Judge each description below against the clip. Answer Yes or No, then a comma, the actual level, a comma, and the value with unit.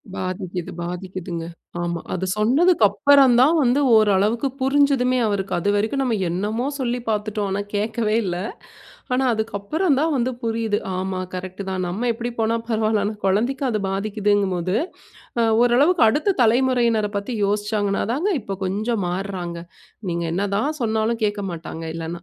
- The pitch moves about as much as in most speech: Yes, average, 4.1 semitones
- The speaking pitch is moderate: No, high, 215 Hz